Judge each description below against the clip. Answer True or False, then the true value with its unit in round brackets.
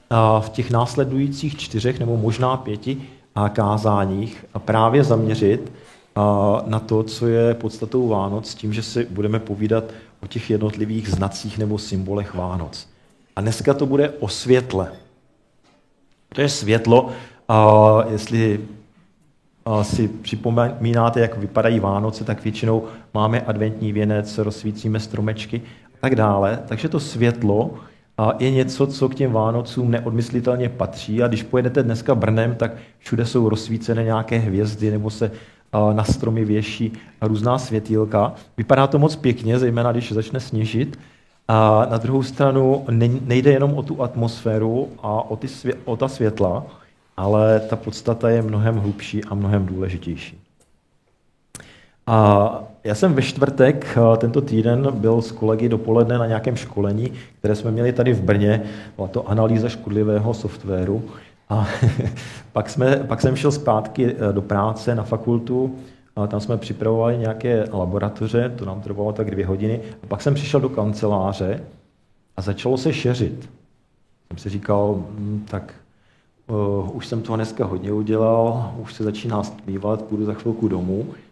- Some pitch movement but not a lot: False (2.3 semitones)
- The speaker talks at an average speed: True (140 wpm)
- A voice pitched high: False (110 Hz)